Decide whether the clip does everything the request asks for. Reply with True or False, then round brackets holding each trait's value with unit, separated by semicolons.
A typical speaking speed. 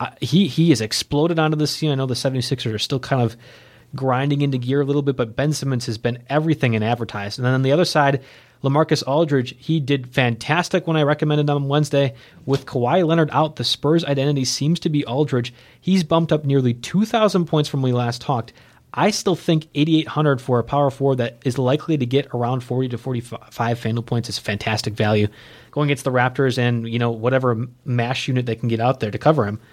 False (225 wpm)